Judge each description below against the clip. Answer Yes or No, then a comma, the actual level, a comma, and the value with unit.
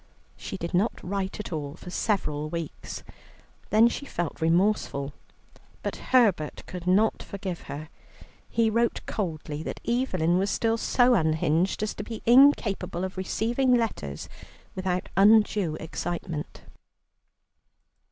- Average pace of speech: No, slow, 125 wpm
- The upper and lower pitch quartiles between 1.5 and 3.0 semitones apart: No, average, 5.2 semitones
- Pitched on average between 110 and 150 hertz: No, high, 190 Hz